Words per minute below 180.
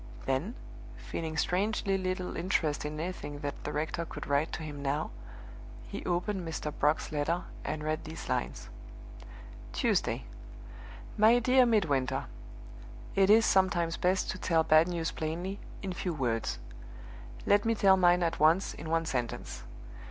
Yes: average, 145 wpm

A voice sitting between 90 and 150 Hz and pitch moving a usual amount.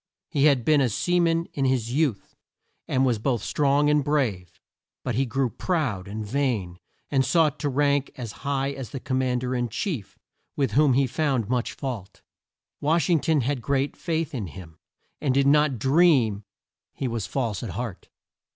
Yes: low, 135 Hz; average, 3.9 semitones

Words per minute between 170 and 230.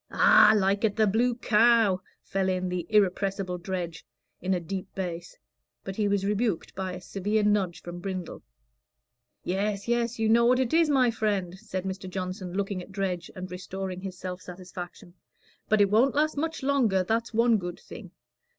Yes: average, 180 wpm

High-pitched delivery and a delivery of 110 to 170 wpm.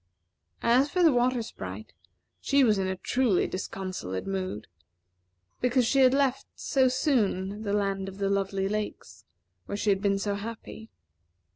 Yes: high, 210 Hz; average, 155 wpm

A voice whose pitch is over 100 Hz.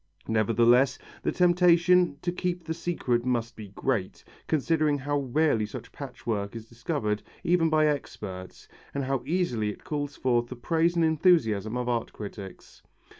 Yes: low, 135 Hz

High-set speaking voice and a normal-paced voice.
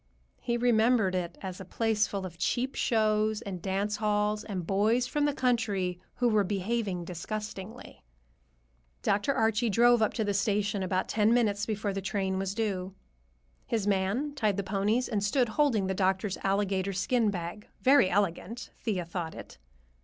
Yes: high, 205 Hz; average, 160 wpm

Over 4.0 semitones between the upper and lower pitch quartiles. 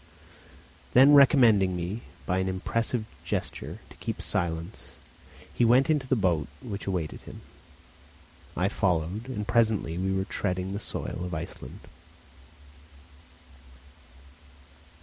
Yes: average, 4.5 semitones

